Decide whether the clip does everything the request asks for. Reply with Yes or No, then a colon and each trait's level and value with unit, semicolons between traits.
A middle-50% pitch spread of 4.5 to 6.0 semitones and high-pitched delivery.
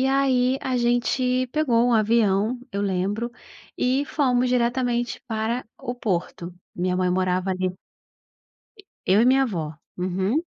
Yes: average, 4.9 semitones; high, 235 Hz